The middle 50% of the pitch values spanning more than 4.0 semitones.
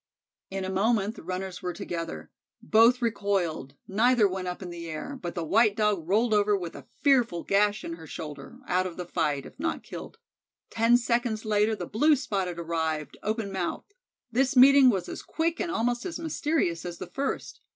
Yes: wide, 5.4 semitones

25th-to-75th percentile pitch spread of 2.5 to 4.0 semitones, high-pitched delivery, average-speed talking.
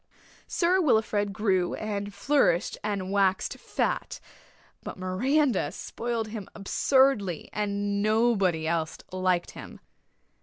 No: average, 3.5 semitones; high, 205 Hz; slow, 105 wpm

